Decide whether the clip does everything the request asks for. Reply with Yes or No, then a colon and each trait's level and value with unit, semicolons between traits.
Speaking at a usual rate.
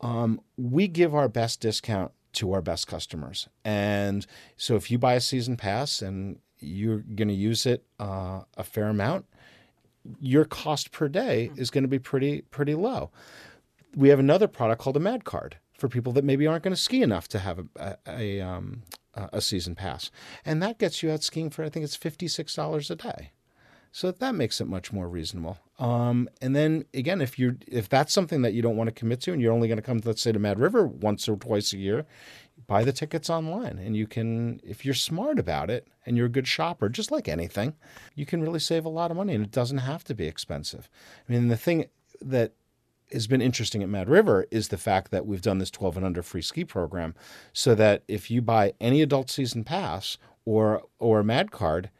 No: fast, 220 wpm